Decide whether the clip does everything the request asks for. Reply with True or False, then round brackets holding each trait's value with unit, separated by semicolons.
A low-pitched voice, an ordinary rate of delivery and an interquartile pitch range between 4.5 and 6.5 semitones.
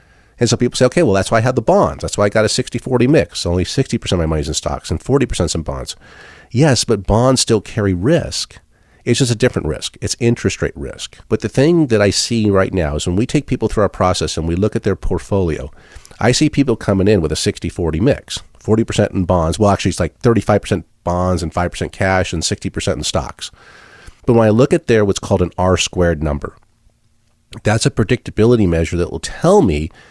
False (100 Hz; 230 wpm; 5.0 semitones)